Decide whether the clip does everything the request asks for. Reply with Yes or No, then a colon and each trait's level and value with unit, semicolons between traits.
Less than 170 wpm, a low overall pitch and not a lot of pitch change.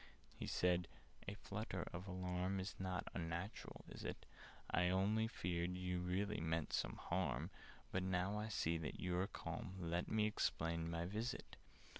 Yes: average, 155 wpm; very low, 90 Hz; narrow, 2.2 semitones